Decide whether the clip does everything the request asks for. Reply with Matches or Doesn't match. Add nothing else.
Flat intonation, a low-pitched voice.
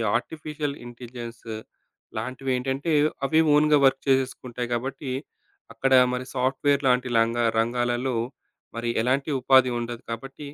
Matches